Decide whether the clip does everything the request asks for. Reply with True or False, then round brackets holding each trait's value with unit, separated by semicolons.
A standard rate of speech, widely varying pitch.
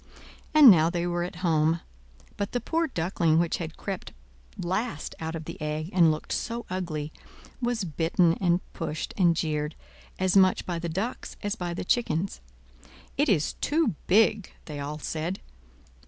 False (165 wpm; 3.7 semitones)